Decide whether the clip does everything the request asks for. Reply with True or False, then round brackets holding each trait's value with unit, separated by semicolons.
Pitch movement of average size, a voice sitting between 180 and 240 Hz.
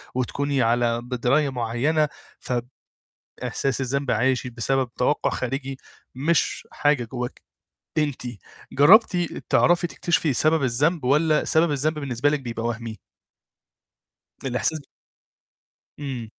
False (3.6 semitones; 135 Hz)